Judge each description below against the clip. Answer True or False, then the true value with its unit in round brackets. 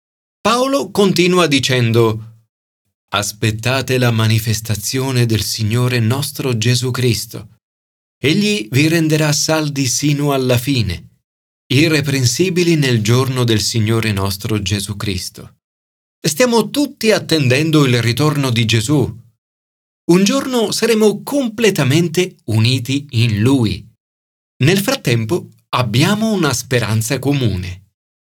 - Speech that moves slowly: True (100 wpm)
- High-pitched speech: False (125 Hz)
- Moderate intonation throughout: False (6.0 semitones)